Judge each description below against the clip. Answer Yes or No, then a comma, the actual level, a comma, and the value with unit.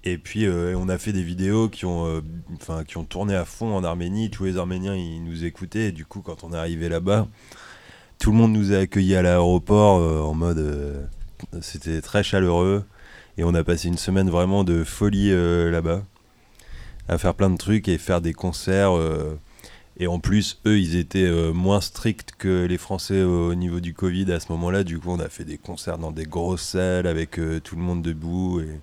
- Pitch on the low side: Yes, very low, 90 Hz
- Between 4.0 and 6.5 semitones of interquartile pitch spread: No, average, 2.8 semitones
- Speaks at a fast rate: Yes, fast, 225 wpm